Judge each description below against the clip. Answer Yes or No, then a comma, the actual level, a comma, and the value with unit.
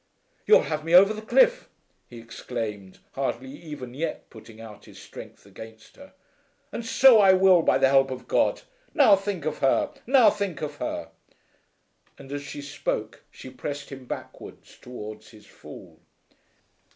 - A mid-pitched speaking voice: Yes, medium, 145 Hz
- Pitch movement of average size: No, wide, 7.9 semitones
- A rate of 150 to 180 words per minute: Yes, average, 160 wpm